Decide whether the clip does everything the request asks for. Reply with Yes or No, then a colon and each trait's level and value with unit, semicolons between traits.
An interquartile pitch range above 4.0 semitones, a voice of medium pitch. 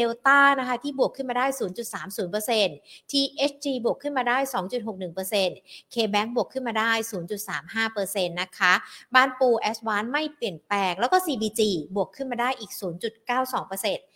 No: average, 4.6 semitones; high, 225 Hz